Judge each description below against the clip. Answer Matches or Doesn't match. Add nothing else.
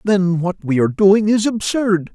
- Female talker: Doesn't match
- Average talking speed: Matches